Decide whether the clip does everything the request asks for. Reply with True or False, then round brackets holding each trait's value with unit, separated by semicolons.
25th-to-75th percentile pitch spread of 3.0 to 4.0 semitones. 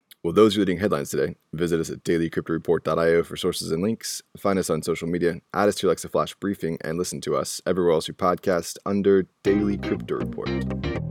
True (3.4 semitones)